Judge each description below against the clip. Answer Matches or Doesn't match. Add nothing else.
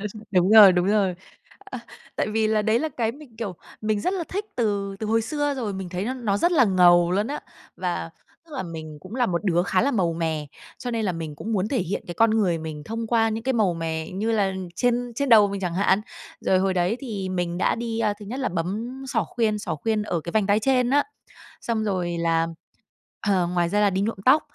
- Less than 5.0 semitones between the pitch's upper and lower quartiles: Matches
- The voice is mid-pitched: Doesn't match